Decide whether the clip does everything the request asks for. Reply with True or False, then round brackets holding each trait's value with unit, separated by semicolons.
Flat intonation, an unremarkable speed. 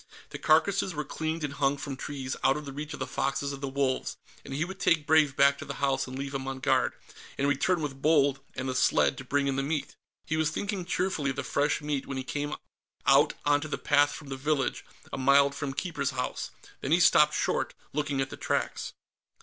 False (1.9 semitones; 230 wpm)